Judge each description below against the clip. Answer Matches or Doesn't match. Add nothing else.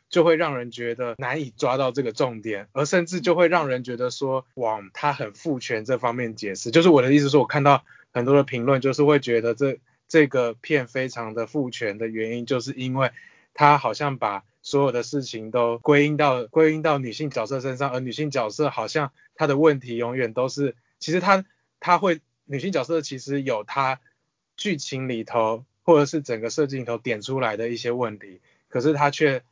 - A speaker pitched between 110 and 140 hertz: Matches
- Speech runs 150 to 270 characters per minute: Doesn't match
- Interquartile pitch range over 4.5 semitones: Doesn't match